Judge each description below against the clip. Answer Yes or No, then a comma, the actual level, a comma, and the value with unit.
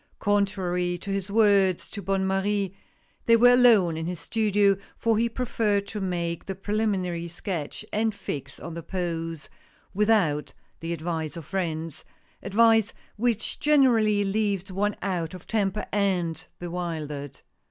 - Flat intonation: No, average, 3.7 semitones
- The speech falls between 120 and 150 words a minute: Yes, average, 145 wpm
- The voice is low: No, high, 195 Hz